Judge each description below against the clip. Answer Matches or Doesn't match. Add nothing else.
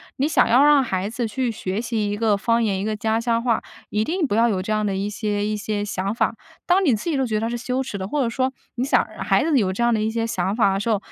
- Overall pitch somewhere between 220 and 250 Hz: Matches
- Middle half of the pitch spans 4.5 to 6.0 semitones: Doesn't match